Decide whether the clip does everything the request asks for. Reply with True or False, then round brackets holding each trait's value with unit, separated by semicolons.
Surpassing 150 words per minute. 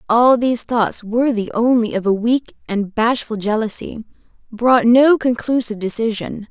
False (140 wpm)